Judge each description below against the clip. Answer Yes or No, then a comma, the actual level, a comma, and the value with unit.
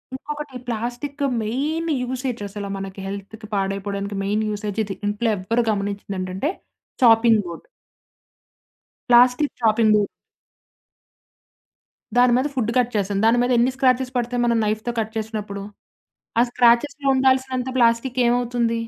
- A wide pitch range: No, average, 3.4 semitones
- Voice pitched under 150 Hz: No, high, 235 Hz